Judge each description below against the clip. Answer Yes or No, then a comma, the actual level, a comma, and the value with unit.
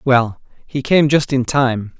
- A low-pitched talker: Yes, low, 130 Hz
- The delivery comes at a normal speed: Yes, average, 180 wpm